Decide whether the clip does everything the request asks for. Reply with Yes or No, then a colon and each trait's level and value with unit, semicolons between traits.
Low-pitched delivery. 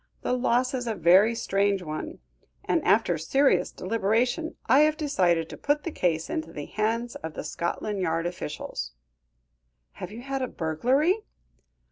No: high, 215 Hz